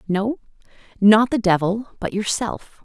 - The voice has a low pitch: No, high, 210 Hz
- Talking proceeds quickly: No, slow, 125 wpm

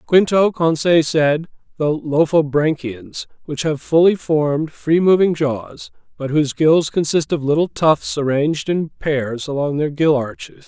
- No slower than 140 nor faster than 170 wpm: Yes, average, 145 wpm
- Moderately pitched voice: Yes, medium, 150 Hz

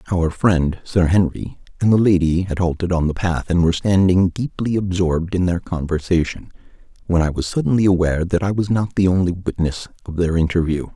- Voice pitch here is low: Yes, very low, 90 Hz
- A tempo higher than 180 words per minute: Yes, average, 190 wpm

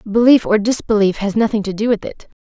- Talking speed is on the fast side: Yes, fast, 225 wpm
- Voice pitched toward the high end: Yes, high, 215 Hz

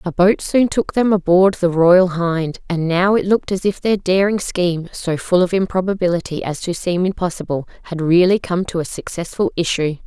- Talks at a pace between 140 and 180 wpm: No, average, 195 wpm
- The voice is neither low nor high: Yes, medium, 180 Hz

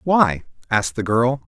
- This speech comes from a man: Yes, male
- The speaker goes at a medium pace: Yes, average, 160 wpm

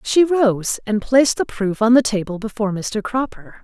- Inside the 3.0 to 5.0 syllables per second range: Yes, 4.9 syllables/s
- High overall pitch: Yes, high, 225 Hz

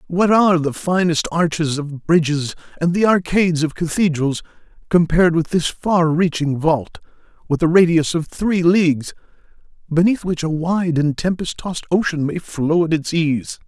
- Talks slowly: No, average, 160 wpm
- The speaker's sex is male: Yes, male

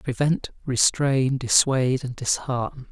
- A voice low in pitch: Yes, low, 130 Hz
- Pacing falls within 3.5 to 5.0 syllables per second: Yes, 4.0 syllables/s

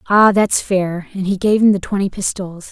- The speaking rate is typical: No, fast, 220 wpm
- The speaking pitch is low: No, high, 195 Hz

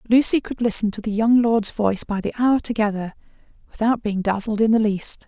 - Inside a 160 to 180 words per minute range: No, average, 195 wpm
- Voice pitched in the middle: No, high, 220 Hz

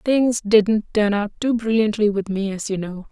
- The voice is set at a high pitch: Yes, high, 210 Hz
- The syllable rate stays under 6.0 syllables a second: Yes, 4.5 syllables/s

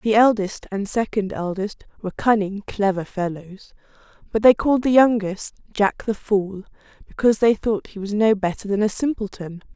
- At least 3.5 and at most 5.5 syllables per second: Yes, 5.0 syllables/s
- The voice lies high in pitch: Yes, high, 205 Hz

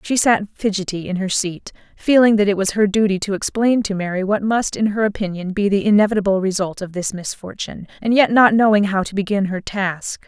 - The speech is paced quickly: Yes, fast, 215 wpm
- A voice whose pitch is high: Yes, high, 200 Hz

